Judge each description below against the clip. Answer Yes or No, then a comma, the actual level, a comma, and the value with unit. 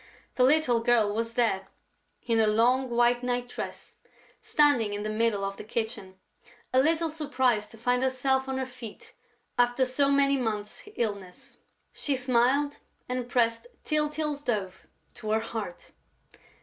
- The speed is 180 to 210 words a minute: No, average, 150 wpm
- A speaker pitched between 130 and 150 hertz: No, high, 245 Hz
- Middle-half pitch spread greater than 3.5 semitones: No, average, 3.1 semitones